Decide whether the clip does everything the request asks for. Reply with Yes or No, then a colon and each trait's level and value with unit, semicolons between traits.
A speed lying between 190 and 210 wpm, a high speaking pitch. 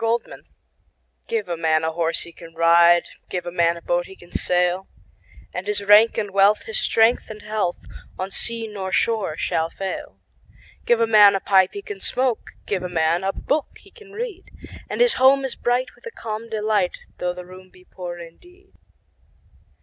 Yes: average, 195 wpm; high, 195 Hz